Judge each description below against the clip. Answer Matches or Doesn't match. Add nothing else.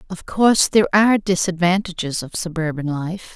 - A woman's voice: Matches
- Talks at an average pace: Matches